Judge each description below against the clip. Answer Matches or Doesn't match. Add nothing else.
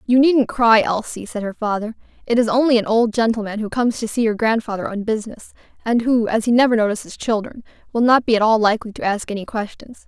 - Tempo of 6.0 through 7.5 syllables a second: Matches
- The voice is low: Doesn't match